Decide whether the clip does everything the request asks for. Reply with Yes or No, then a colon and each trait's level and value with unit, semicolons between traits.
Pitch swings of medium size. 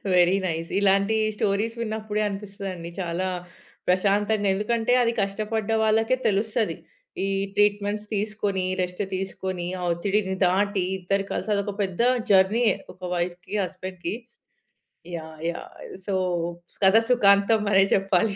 No: narrow, 2.2 semitones